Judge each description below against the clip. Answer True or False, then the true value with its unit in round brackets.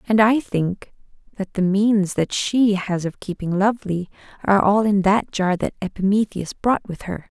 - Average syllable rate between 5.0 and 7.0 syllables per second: False (4.6 syllables/s)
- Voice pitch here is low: False (200 Hz)